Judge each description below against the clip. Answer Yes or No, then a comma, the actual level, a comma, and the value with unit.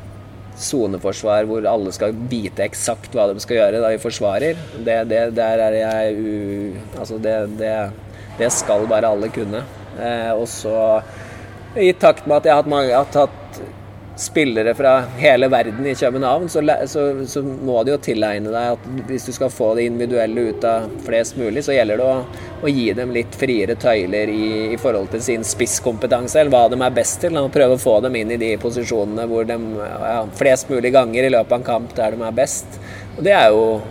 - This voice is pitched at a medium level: No, low, 115 Hz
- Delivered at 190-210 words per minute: Yes, fast, 205 wpm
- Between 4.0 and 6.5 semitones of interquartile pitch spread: No, average, 2.8 semitones